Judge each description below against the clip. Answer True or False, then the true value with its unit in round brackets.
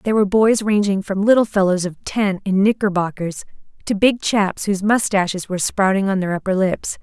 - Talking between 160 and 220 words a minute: True (190 wpm)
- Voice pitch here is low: False (200 Hz)